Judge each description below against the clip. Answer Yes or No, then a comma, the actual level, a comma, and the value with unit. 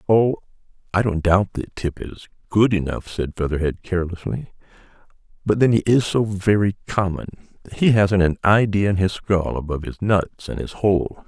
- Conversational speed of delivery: Yes, average, 170 wpm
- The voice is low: Yes, very low, 95 Hz